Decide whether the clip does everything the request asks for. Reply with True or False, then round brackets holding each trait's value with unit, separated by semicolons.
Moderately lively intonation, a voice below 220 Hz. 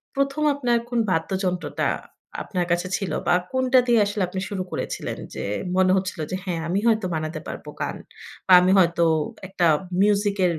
True (3.8 semitones; 190 Hz)